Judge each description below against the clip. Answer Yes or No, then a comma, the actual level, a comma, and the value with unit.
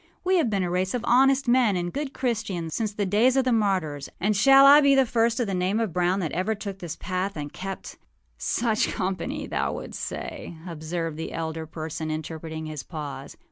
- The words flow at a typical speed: No, fast, 210 wpm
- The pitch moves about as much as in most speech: No, wide, 6.4 semitones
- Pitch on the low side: No, high, 190 Hz